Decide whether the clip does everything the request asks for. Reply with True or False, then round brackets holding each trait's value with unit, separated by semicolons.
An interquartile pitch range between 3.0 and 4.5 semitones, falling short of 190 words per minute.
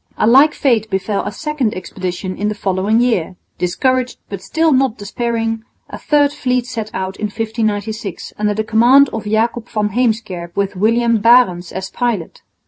True (3.5 semitones; 165 wpm)